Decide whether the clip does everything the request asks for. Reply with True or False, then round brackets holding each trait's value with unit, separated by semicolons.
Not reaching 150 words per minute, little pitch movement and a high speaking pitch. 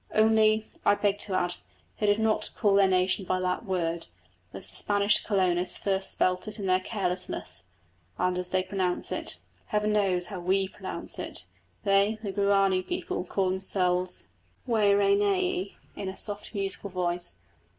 False (170 wpm; 2.0 semitones; 195 Hz)